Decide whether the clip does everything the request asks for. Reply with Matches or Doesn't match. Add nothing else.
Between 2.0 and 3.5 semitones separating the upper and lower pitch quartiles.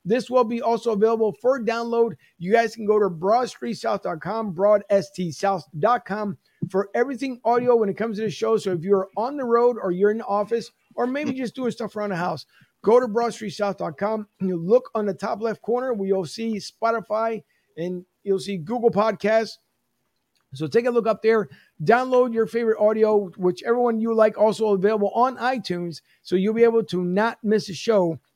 Matches